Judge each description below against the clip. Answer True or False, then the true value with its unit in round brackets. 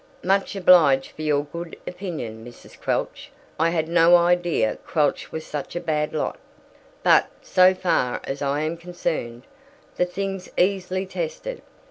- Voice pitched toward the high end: False (170 Hz)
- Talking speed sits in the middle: True (145 wpm)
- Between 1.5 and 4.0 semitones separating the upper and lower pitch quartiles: True (3.5 semitones)